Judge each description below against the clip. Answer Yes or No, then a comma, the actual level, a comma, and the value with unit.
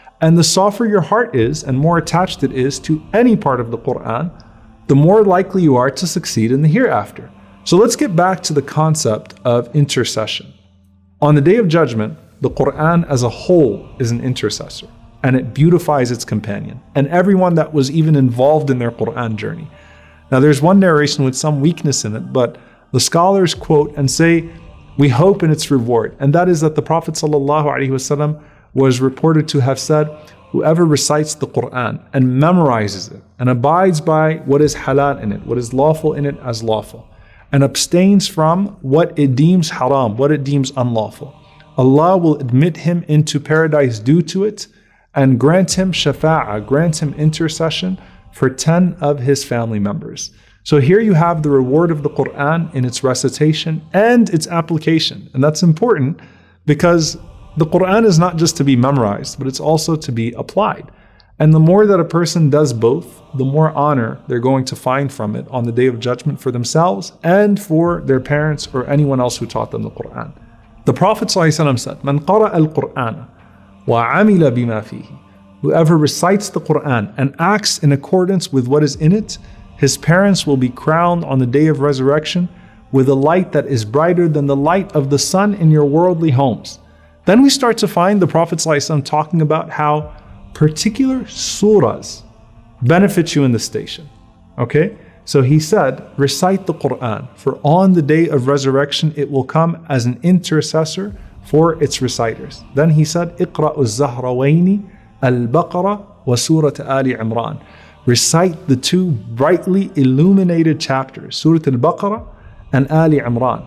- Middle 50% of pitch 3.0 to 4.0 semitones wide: No, average, 4.5 semitones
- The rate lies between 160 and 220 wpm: Yes, average, 175 wpm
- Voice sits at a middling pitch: Yes, medium, 150 Hz